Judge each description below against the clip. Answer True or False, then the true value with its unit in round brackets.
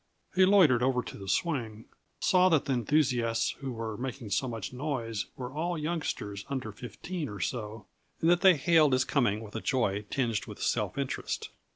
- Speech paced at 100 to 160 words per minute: False (185 wpm)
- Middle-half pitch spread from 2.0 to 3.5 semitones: False (5.4 semitones)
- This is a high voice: False (125 Hz)